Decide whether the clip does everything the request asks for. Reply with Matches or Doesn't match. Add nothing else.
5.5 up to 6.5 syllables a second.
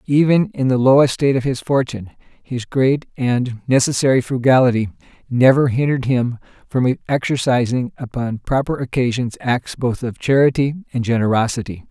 Doesn't match